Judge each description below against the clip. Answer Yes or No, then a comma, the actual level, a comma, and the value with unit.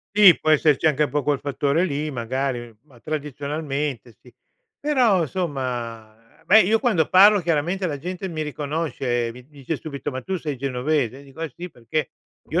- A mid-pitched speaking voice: Yes, medium, 145 Hz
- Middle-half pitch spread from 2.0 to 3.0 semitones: No, average, 4.1 semitones